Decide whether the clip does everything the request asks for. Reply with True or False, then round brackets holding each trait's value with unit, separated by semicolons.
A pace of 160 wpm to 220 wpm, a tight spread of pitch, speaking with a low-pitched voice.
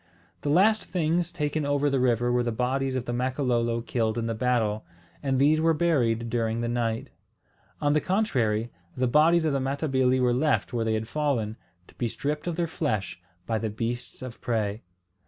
False (190 wpm; 4.2 semitones; 125 Hz)